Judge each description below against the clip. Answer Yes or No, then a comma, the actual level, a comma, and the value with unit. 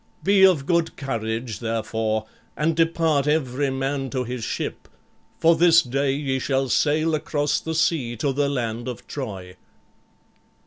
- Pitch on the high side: No, low, 135 Hz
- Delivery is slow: No, average, 145 wpm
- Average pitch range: Yes, average, 4.6 semitones